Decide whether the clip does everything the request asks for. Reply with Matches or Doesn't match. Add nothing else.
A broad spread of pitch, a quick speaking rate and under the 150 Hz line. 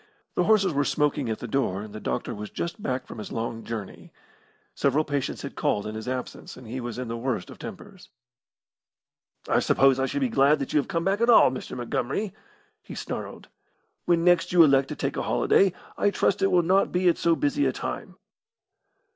Matches